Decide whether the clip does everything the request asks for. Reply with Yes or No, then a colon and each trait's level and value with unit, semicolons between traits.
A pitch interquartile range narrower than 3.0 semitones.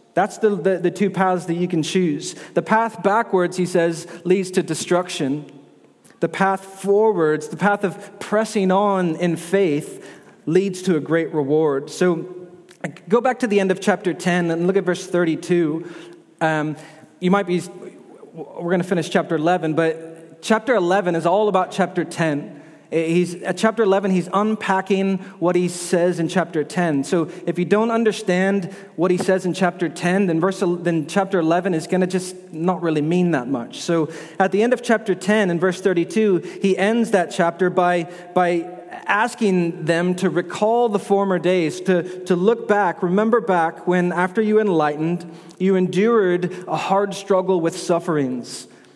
Yes: narrow, 2.4 semitones